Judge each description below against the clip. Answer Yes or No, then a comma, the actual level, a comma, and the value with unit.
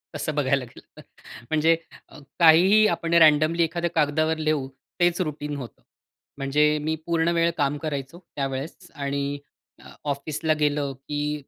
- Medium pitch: Yes, medium, 150 Hz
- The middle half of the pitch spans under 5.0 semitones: Yes, narrow, 2.6 semitones